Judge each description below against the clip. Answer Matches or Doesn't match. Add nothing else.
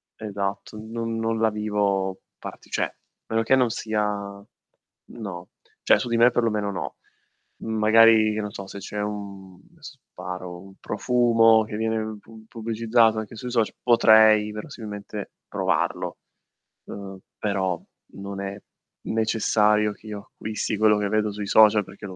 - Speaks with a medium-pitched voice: Doesn't match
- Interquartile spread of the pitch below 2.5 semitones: Matches